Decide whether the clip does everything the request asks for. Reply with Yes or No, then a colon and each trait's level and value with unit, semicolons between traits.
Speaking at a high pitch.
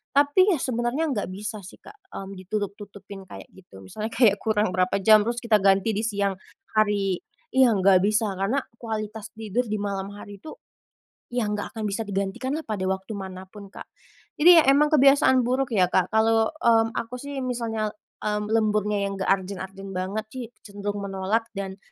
Yes: high, 210 Hz